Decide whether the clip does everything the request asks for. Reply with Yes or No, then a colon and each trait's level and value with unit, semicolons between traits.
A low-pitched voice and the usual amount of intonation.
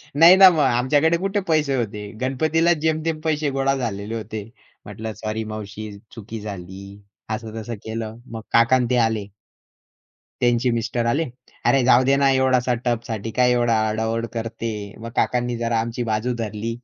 Yes: low, 120 Hz; average, 3.3 semitones